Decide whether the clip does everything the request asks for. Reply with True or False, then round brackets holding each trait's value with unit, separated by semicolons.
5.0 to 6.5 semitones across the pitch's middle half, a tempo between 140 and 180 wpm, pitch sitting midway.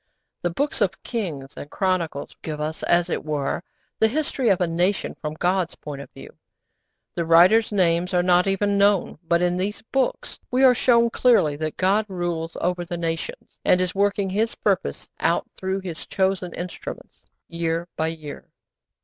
False (3.4 semitones; 175 wpm; 180 Hz)